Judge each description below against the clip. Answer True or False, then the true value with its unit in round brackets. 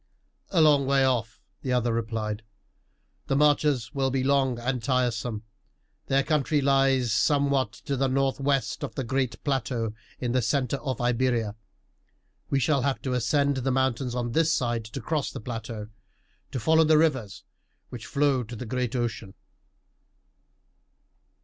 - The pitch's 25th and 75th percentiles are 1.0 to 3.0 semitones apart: True (2.7 semitones)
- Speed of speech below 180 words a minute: True (150 wpm)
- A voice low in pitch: True (130 Hz)